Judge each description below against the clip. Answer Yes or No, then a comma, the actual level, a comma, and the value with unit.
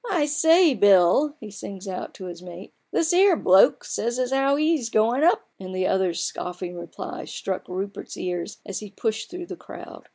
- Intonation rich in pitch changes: Yes, wide, 8.4 semitones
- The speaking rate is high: Yes, fast, 220 wpm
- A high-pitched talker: Yes, high, 215 Hz